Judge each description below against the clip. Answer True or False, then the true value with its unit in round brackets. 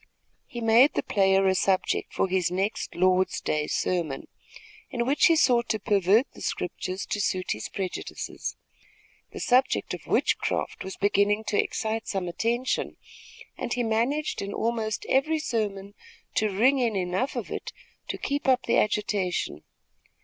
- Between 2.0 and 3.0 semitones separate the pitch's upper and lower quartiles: False (4.0 semitones)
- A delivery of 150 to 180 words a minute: True (155 wpm)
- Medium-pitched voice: False (210 Hz)